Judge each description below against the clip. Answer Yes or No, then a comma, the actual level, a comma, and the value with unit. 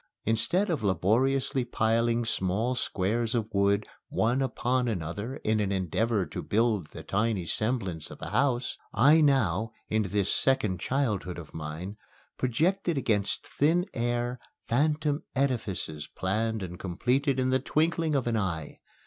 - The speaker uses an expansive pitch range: No, average, 5.0 semitones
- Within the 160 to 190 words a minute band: No, average, 140 wpm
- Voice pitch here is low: Yes, low, 115 Hz